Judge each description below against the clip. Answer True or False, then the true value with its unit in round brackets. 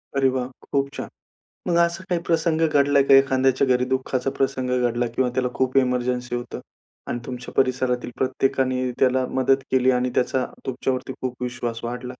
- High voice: False (130 Hz)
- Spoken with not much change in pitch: True (1.3 semitones)